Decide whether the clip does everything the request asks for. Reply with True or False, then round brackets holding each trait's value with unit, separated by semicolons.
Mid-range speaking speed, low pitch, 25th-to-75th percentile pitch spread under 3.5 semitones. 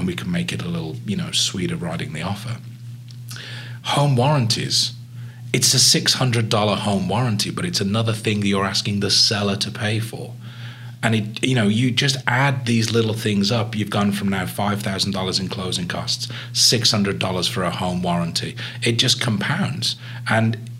True (190 wpm; 115 Hz; 2.9 semitones)